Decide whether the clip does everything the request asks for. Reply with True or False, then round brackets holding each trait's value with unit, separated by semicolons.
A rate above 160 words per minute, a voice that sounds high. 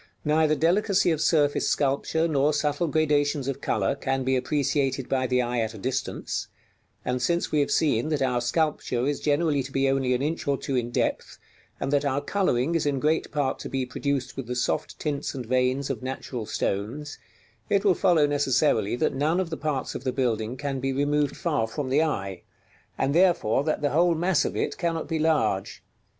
False (200 wpm; 140 Hz)